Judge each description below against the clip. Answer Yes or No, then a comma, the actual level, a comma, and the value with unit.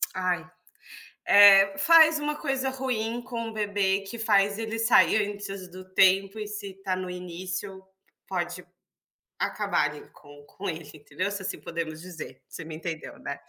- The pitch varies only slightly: No, average, 3.4 semitones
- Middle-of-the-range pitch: No, high, 195 Hz